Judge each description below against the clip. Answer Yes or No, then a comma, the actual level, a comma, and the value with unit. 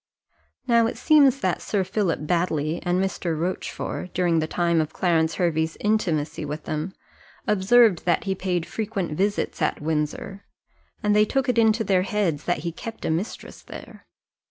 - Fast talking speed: No, average, 165 wpm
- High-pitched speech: No, medium, 180 Hz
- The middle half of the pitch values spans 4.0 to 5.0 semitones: Yes, average, 4.6 semitones